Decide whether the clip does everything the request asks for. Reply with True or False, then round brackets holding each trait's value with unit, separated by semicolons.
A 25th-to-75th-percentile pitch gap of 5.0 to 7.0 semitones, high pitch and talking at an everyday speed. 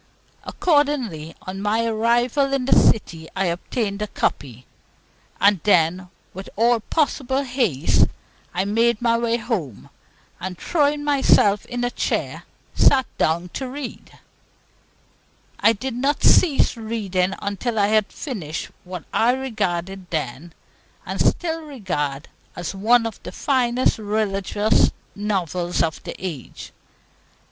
False (5.4 semitones; 215 Hz; 130 wpm)